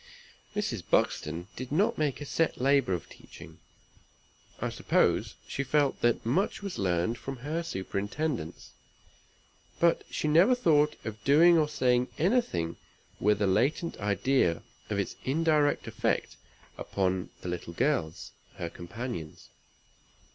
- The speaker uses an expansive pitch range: Yes, wide, 8.2 semitones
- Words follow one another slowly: Yes, slow, 130 wpm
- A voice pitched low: Yes, low, 130 Hz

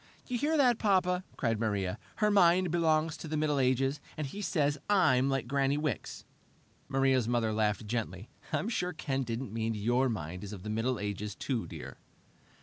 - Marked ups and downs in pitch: Yes, wide, 6.5 semitones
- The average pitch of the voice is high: No, low, 135 Hz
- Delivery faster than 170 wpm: Yes, average, 180 wpm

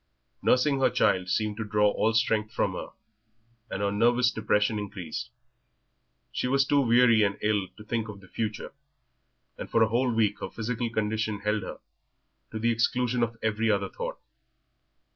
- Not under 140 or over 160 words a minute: No, average, 170 wpm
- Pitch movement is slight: Yes, narrow, 2.1 semitones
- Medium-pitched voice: No, low, 110 Hz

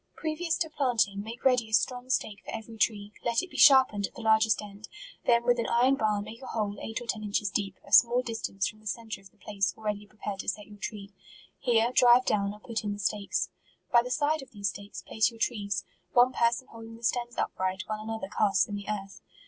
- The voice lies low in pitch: No, high, 220 Hz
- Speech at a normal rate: No, fast, 235 wpm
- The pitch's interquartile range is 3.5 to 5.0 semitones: No, average, 2.8 semitones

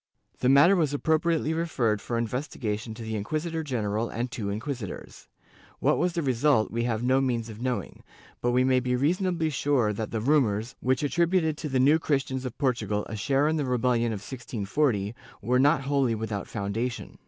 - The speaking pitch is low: Yes, low, 125 Hz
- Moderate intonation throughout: Yes, average, 4.6 semitones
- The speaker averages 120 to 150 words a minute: No, average, 185 wpm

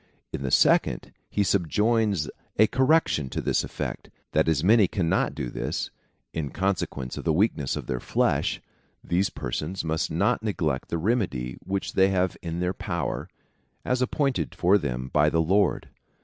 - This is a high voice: No, very low, 90 Hz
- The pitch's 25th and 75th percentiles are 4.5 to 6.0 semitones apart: Yes, average, 5.2 semitones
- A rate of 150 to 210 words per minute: Yes, average, 165 wpm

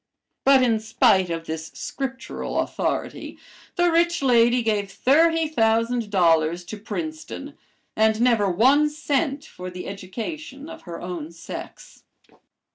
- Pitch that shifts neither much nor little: No, wide, 7.4 semitones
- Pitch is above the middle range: Yes, high, 230 Hz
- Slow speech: Yes, slow, 125 wpm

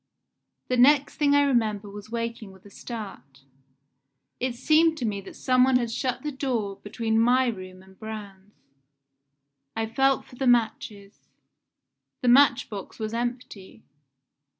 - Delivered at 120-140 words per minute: No, average, 150 wpm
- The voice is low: No, high, 230 Hz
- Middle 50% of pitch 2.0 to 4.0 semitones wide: Yes, average, 3.7 semitones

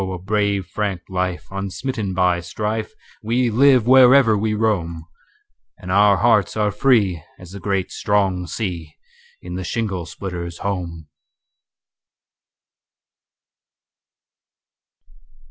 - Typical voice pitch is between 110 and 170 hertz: No, low, 100 Hz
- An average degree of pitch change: Yes, average, 3.3 semitones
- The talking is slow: Yes, slow, 95 wpm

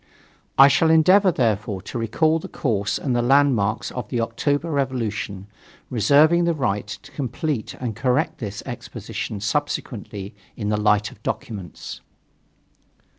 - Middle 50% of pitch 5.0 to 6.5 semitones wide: Yes, wide, 5.5 semitones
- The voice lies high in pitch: No, low, 120 Hz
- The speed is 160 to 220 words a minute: No, slow, 135 wpm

